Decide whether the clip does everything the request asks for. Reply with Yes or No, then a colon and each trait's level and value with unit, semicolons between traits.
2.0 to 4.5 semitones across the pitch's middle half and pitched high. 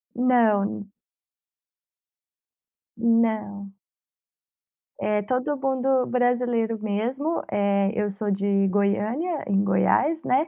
Yes: average, 3.9 semitones; high, 225 Hz